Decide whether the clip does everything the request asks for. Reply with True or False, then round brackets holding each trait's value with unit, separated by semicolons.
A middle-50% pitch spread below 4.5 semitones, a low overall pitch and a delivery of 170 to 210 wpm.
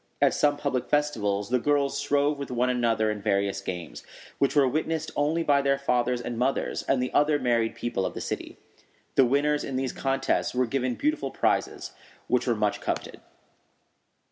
True (3.3 semitones; 130 Hz; 180 wpm)